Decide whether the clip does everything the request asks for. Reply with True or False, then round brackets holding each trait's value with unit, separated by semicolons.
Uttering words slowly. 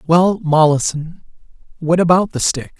True (110 wpm)